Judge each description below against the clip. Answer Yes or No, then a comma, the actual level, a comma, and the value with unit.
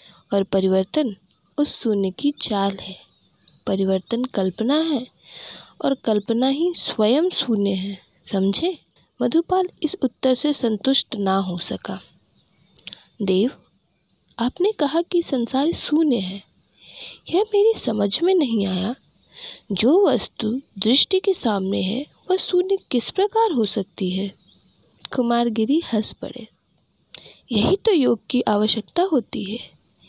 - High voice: Yes, high, 240 Hz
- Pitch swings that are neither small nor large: No, wide, 7.3 semitones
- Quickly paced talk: No, average, 120 wpm